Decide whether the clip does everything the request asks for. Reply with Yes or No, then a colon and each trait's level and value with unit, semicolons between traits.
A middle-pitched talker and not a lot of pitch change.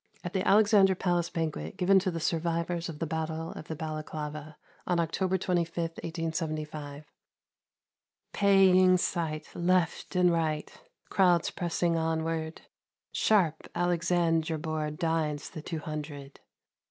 Yes: medium, 165 Hz; narrow, 2.2 semitones